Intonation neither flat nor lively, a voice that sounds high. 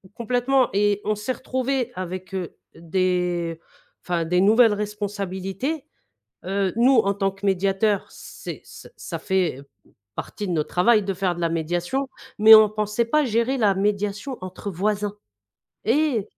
Yes: average, 3.6 semitones; high, 205 Hz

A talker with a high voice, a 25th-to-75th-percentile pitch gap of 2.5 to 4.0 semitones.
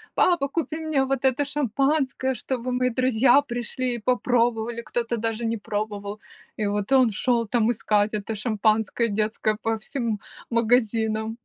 Yes: high, 235 Hz; average, 2.9 semitones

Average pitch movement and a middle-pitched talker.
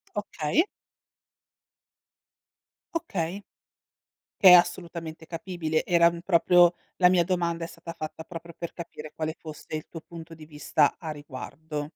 No: narrow, 1.9 semitones; medium, 170 Hz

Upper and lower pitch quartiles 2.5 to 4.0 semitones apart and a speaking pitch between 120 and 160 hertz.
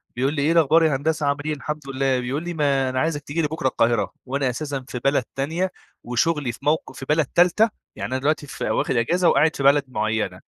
Yes: average, 3.3 semitones; medium, 140 Hz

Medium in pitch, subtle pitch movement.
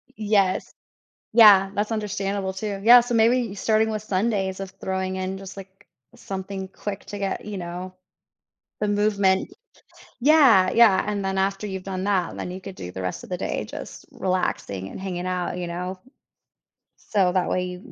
No: high, 195 Hz; narrow, 1.9 semitones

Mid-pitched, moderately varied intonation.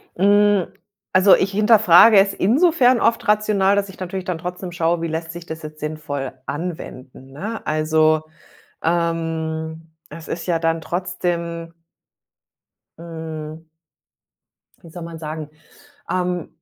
Yes: medium, 170 Hz; average, 3.2 semitones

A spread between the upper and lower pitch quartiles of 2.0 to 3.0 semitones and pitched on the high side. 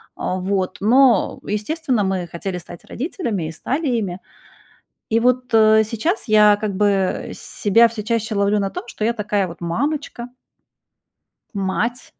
No: average, 3.5 semitones; high, 210 Hz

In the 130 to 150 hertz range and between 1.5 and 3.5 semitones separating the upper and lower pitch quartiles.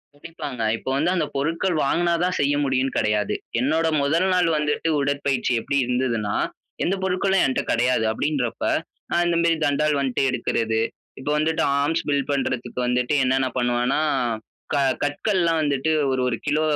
No: medium, 140 Hz; average, 4.3 semitones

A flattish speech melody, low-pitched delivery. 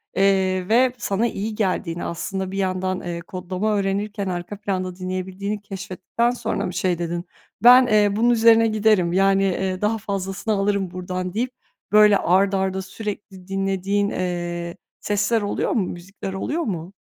No: narrow, 2.3 semitones; high, 195 Hz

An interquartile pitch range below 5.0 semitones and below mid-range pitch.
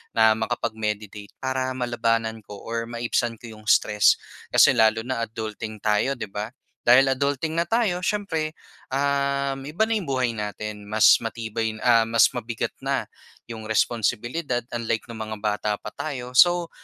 Yes: average, 3.7 semitones; low, 115 Hz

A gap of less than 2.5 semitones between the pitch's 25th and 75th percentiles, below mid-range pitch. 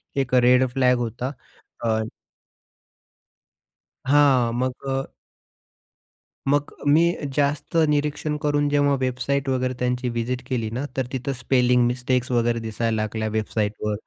No: average, 2.8 semitones; low, 125 Hz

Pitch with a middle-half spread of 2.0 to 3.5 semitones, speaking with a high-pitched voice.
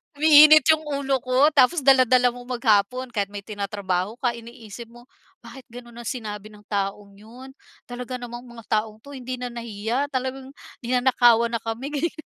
Yes: average, 3.0 semitones; high, 245 Hz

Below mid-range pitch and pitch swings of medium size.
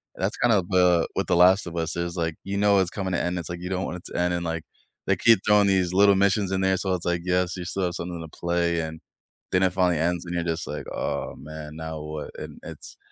No: very low, 90 Hz; narrow, 1.9 semitones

